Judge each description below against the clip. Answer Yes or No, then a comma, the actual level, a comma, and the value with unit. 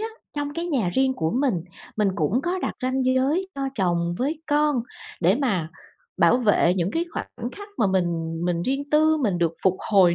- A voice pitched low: No, very high, 250 Hz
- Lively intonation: Yes, wide, 8.6 semitones